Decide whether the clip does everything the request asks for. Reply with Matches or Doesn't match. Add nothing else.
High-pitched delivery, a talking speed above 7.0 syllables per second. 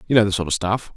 Doesn't match